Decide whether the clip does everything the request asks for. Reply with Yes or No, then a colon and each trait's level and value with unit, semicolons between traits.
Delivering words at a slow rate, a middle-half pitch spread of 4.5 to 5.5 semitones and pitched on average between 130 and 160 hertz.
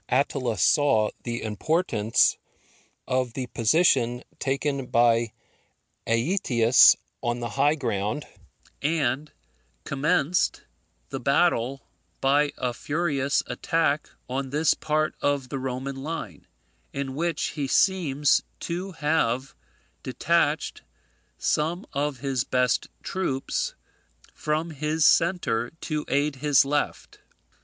No: slow, 105 wpm; average, 3.6 semitones; medium, 140 Hz